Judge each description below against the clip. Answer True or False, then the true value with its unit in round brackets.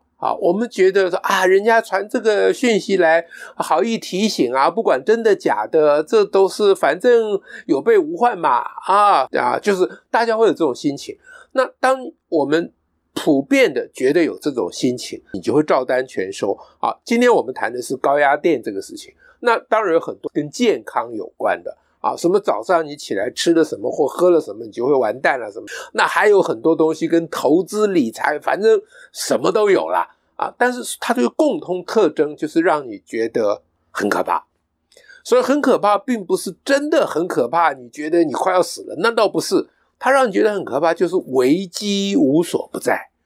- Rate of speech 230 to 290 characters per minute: True (280 characters per minute)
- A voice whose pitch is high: True (245 Hz)